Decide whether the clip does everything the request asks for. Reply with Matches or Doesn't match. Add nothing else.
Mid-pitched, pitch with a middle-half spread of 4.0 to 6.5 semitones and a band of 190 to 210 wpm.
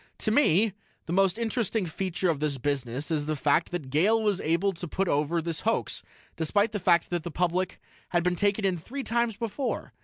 Matches